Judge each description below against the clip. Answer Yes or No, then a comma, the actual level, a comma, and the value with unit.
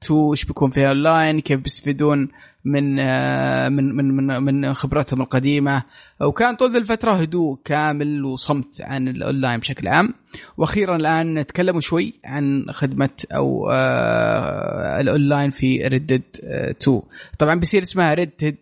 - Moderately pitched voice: Yes, medium, 145 Hz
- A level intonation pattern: No, average, 3.0 semitones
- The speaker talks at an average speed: Yes, average, 120 wpm